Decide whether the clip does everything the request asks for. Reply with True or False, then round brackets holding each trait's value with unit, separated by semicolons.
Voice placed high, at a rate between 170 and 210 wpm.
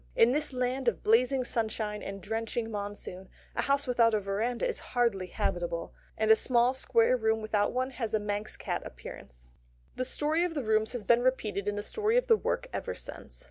True (225 Hz; 200 wpm)